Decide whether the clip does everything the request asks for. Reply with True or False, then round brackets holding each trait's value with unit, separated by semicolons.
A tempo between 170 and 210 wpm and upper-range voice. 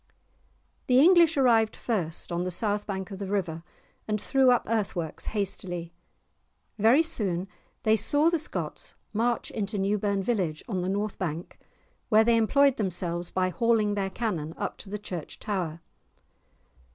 False (155 wpm; 205 Hz)